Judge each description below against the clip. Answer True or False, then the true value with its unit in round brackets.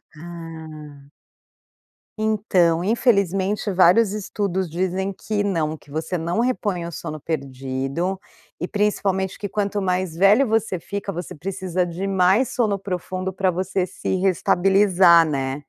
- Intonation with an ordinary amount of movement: True (3.0 semitones)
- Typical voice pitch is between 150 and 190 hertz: True (185 Hz)